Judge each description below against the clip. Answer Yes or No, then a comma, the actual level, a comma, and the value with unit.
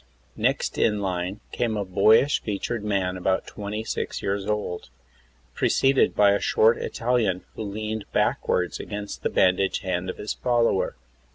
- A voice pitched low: Yes, low, 100 Hz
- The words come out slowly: No, average, 145 wpm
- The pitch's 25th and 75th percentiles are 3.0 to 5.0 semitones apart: No, narrow, 2.6 semitones